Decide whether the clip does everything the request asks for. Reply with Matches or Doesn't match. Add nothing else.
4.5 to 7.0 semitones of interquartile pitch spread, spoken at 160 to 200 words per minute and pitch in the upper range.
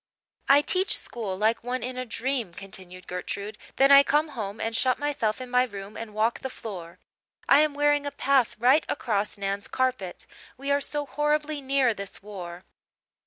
Matches